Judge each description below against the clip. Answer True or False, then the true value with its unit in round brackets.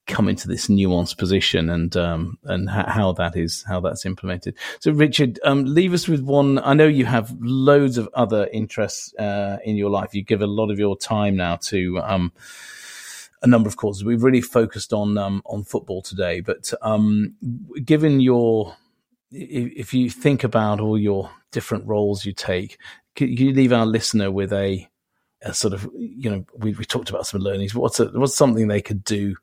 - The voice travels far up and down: False (3.9 semitones)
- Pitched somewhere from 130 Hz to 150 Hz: False (110 Hz)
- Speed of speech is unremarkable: True (195 wpm)